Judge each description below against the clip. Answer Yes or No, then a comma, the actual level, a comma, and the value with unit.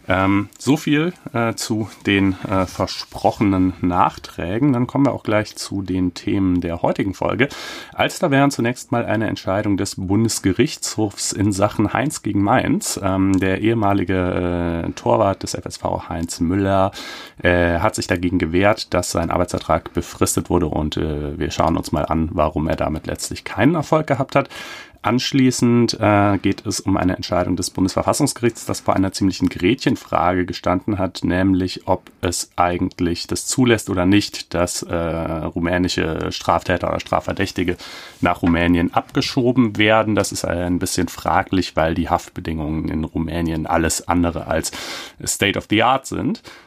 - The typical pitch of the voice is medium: No, very low, 95 Hz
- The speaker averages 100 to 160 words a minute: Yes, average, 155 wpm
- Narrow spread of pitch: No, average, 3.7 semitones